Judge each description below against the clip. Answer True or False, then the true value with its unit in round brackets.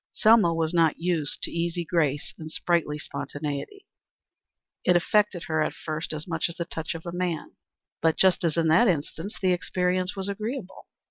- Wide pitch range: False (2.5 semitones)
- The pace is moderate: True (170 wpm)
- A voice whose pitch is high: False (170 Hz)